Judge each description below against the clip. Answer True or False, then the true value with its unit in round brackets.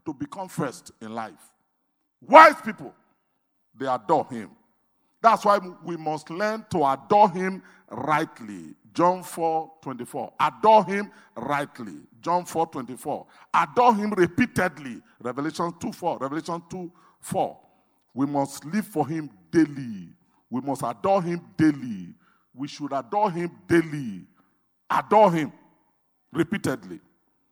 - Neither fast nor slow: False (120 wpm)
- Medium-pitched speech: True (175 Hz)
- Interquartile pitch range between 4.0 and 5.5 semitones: True (4.8 semitones)